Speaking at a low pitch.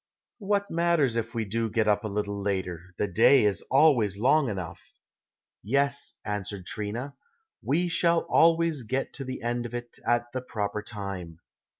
Yes: low, 115 Hz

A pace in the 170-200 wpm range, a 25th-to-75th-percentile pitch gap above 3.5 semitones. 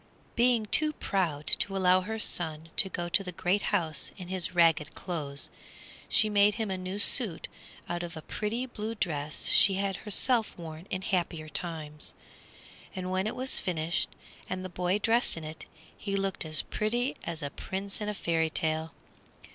Yes: average, 180 wpm; average, 4.1 semitones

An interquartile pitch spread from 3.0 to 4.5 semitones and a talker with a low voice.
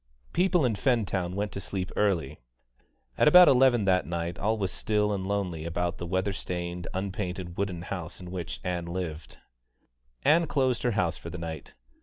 Yes: average, 3.3 semitones; very low, 95 Hz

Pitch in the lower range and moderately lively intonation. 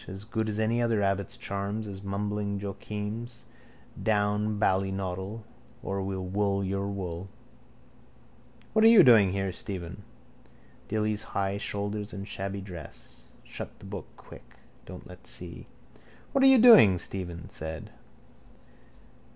No: low, 100 Hz; narrow, 1.7 semitones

